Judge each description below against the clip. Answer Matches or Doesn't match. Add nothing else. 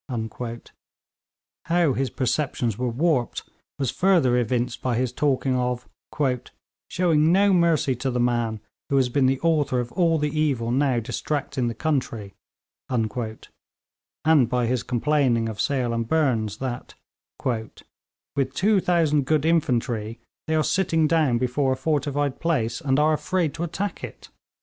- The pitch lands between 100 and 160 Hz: Matches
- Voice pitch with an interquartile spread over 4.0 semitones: Matches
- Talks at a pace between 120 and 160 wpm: Matches